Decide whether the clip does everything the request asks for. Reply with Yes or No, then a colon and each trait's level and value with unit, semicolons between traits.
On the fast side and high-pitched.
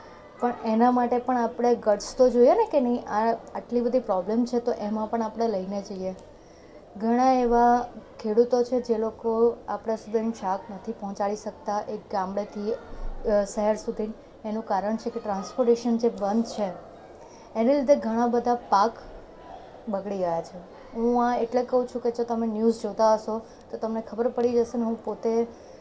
Yes: fast, 170 wpm; high, 230 Hz